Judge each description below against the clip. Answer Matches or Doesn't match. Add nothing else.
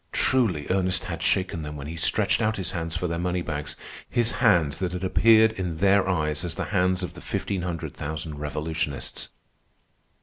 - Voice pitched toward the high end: Doesn't match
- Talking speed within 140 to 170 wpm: Doesn't match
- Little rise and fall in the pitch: Doesn't match